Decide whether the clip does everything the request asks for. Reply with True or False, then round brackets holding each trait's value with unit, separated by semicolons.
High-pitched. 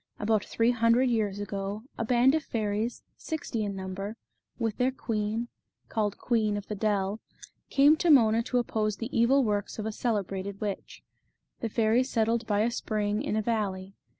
True (220 Hz)